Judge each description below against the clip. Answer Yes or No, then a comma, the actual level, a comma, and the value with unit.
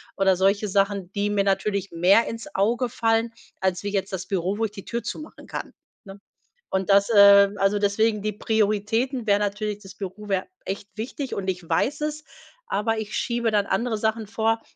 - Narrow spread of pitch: Yes, narrow, 2.3 semitones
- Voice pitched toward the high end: Yes, high, 205 Hz